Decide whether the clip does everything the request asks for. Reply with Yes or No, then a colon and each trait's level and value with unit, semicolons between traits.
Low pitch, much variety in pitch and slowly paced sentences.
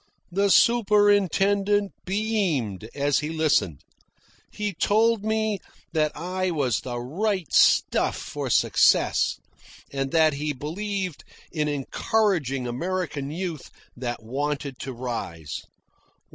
No: medium, 160 Hz; wide, 6.8 semitones; slow, 105 wpm